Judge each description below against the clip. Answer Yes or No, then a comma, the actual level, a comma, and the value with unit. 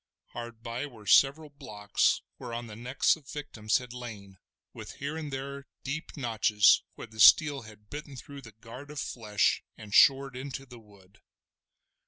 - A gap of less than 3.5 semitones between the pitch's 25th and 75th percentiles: No, average, 4.5 semitones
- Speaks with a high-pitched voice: No, low, 120 Hz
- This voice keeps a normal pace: Yes, average, 170 wpm